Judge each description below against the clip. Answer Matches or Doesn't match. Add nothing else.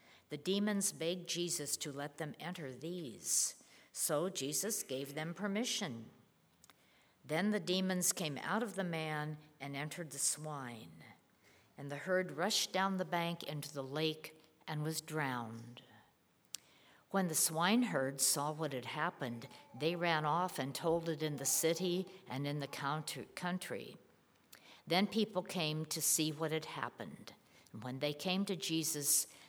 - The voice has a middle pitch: Matches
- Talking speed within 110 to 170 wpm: Matches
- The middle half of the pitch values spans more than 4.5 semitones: Doesn't match